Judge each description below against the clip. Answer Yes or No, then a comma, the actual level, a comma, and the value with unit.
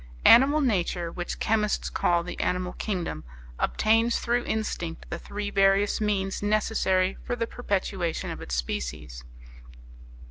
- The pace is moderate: No, slow, 130 wpm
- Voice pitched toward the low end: No, high, 195 Hz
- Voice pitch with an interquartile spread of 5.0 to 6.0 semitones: No, average, 3.9 semitones